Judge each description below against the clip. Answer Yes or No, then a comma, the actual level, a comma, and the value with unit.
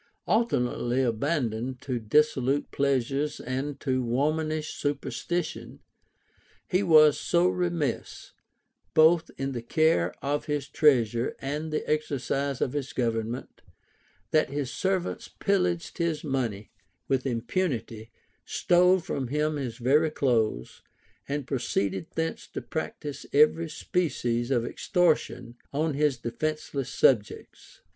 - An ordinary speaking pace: No, slow, 115 wpm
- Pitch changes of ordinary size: Yes, average, 4.2 semitones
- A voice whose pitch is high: No, medium, 140 Hz